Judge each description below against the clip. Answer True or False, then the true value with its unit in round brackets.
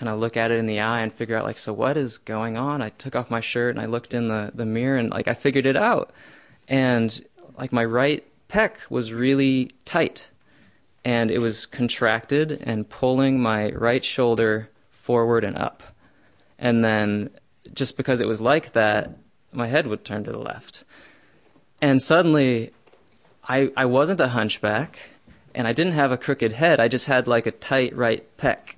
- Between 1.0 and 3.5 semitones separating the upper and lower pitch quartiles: True (2.9 semitones)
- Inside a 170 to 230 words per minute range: True (190 wpm)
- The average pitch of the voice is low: True (120 Hz)